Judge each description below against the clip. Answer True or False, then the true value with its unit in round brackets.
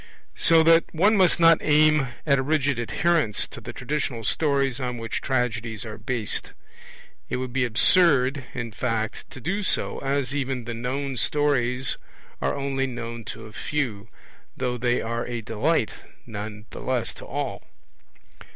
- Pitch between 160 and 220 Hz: False (130 Hz)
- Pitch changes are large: False (3.8 semitones)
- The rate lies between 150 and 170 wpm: True (160 wpm)